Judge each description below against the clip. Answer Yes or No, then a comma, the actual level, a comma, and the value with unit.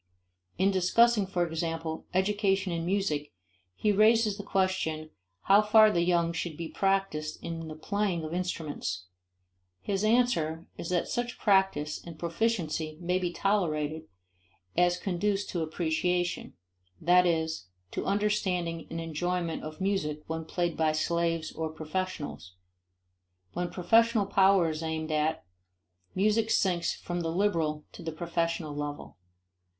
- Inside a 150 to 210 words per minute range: No, slow, 135 wpm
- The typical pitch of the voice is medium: Yes, medium, 175 Hz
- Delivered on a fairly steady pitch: No, average, 3.5 semitones